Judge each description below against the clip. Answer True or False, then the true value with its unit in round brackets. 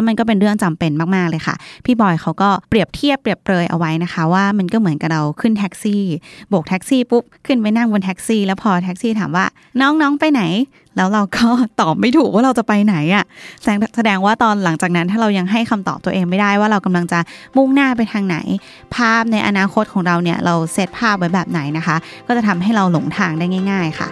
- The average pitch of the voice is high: True (200 Hz)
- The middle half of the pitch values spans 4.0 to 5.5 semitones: True (4.5 semitones)